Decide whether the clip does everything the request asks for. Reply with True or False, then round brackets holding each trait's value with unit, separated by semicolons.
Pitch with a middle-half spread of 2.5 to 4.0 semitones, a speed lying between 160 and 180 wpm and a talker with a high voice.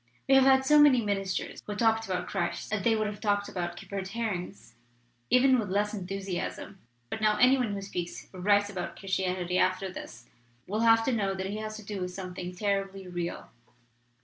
False (2.8 semitones; 200 wpm; 200 Hz)